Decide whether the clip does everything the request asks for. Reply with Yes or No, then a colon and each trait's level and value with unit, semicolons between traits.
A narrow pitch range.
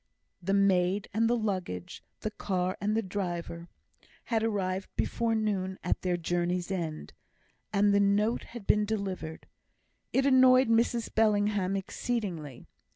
No: average, 3.2 semitones